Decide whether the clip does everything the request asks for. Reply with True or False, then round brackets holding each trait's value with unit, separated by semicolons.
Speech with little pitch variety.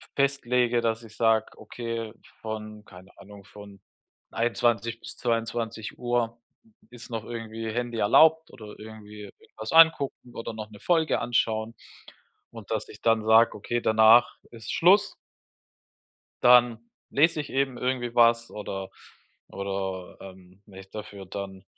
True (2.3 semitones)